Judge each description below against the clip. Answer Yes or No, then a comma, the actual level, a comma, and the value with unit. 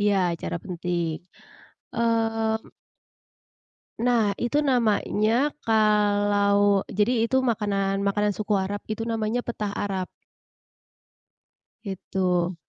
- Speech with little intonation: Yes, narrow, 2.1 semitones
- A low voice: No, high, 210 Hz